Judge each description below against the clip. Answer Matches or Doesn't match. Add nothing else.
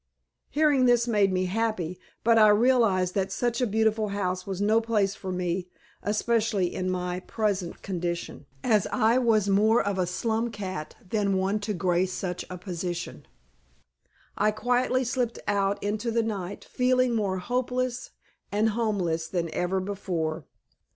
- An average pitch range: Matches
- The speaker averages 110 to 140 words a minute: Doesn't match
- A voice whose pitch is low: Doesn't match